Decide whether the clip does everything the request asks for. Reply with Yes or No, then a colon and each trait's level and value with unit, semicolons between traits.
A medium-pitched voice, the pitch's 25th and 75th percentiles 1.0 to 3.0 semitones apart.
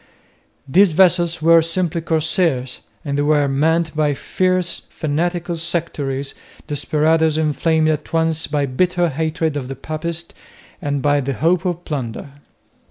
Yes: medium, 160 Hz; average, 2.7 semitones